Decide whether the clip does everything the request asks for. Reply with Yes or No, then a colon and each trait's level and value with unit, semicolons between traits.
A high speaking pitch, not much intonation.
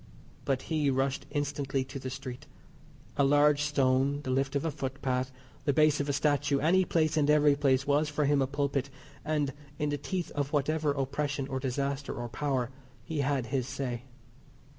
No: medium, 140 Hz; narrow, 1.6 semitones